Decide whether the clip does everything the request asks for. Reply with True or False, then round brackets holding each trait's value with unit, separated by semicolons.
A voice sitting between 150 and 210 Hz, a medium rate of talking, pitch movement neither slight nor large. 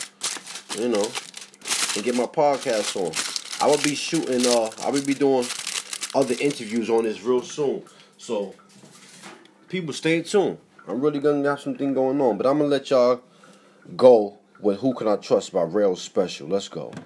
False (135 Hz; 170 wpm; 3.4 semitones)